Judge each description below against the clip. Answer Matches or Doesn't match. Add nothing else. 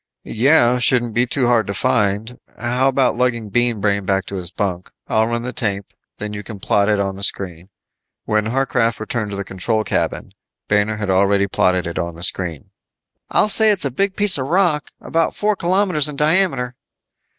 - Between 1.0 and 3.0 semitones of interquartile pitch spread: Doesn't match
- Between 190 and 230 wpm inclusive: Matches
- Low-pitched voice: Matches